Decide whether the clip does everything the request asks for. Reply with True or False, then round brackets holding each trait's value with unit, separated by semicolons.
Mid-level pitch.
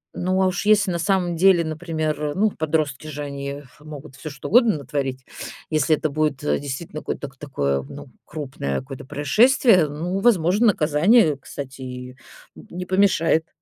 True (155 Hz)